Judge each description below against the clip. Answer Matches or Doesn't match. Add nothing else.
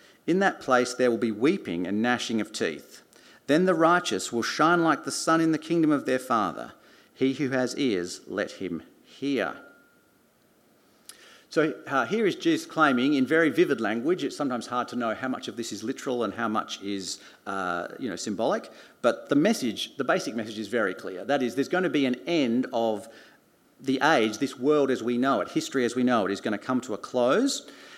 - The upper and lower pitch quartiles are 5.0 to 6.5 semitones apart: Matches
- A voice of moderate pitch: Doesn't match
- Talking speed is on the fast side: Matches